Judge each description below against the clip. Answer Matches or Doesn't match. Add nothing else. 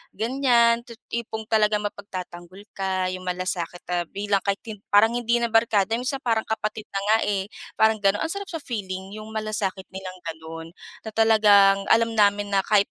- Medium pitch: Doesn't match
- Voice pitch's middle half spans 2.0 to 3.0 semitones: Matches